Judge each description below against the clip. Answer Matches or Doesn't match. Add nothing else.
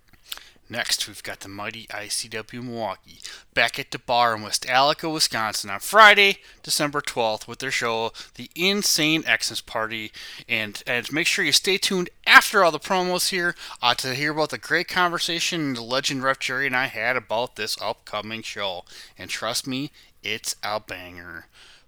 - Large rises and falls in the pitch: Matches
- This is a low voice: Matches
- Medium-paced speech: Matches